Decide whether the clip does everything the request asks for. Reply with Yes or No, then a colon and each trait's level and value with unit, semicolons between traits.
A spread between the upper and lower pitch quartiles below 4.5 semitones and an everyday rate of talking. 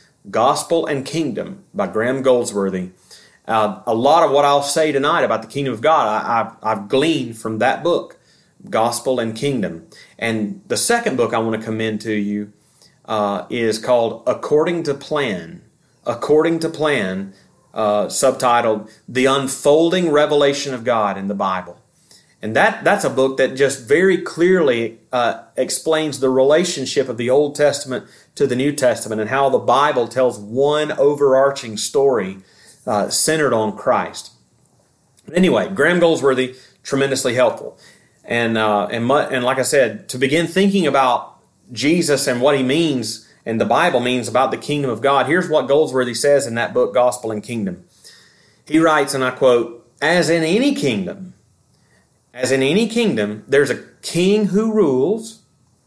No: average, 5.1 semitones; average, 160 wpm